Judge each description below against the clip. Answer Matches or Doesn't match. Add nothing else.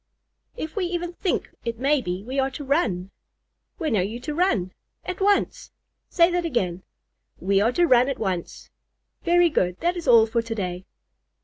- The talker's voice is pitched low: Doesn't match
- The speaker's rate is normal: Matches